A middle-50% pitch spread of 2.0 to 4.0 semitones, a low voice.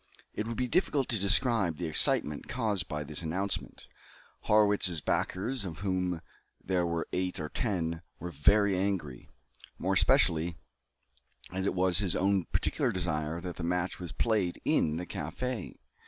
Yes: average, 3.5 semitones; very low, 90 Hz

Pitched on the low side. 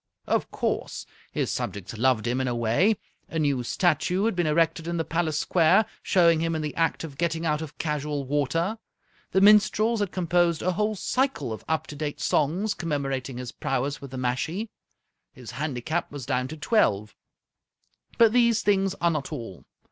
No: medium, 155 Hz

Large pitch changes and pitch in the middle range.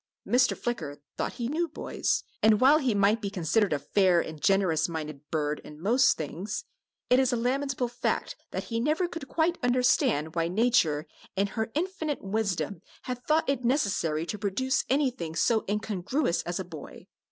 No: wide, 7.1 semitones; high, 215 Hz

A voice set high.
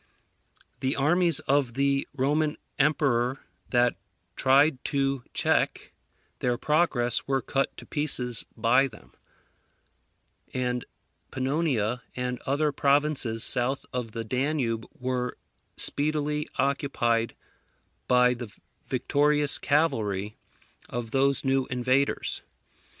No: low, 135 Hz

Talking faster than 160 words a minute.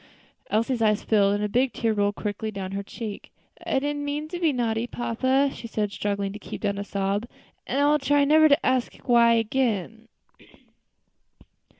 Yes: average, 190 wpm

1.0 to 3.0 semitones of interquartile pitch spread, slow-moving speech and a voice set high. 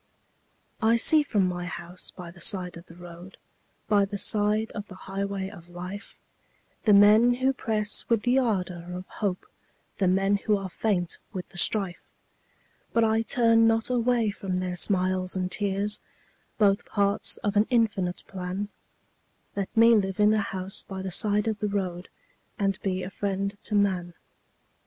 No: narrow, 2.6 semitones; average, 170 wpm; high, 200 Hz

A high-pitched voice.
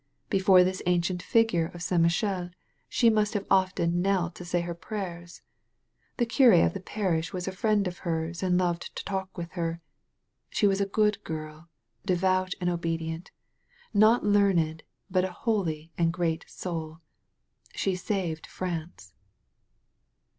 No: medium, 180 Hz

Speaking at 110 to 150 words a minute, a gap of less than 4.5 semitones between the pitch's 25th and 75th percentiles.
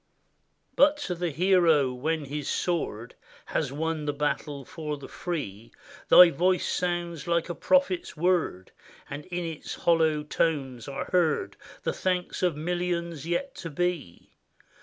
Yes: average, 140 wpm; average, 3.4 semitones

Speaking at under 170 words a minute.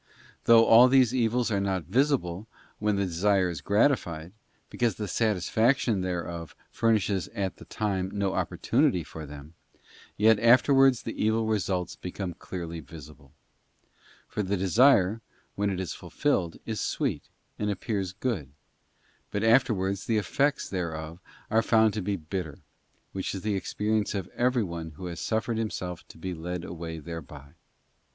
Yes: average, 150 wpm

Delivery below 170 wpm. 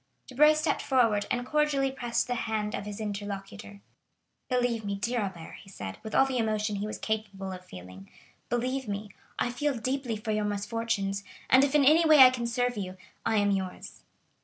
No: average, 185 wpm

